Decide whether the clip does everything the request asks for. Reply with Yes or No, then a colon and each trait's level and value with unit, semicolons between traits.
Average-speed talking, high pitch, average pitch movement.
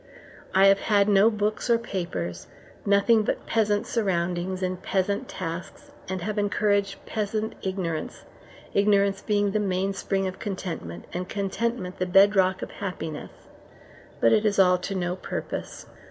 No: average, 145 wpm; high, 195 Hz; narrow, 2.1 semitones